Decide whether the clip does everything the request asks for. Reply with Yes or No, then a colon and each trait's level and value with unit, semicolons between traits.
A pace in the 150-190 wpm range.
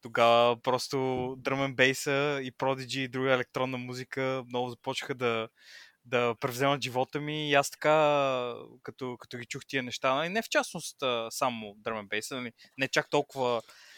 Yes: average, 155 wpm